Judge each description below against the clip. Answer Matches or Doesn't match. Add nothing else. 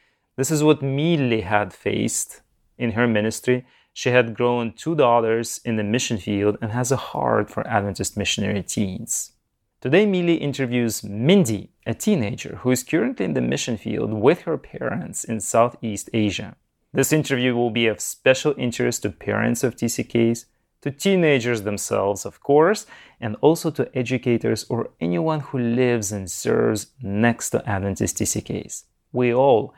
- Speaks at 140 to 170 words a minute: Matches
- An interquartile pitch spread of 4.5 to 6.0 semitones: Doesn't match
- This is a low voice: Matches